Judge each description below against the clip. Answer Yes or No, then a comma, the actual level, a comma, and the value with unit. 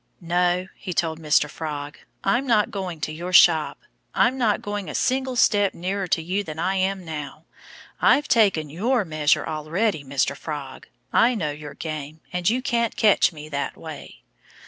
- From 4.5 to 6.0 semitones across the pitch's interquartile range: Yes, average, 5.1 semitones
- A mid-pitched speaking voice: Yes, medium, 175 Hz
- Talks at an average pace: Yes, average, 170 wpm